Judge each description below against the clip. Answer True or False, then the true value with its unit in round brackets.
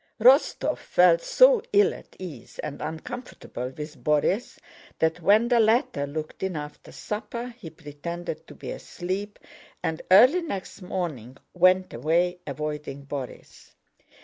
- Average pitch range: False (6.2 semitones)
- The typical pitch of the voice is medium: True (175 Hz)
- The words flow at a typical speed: False (130 wpm)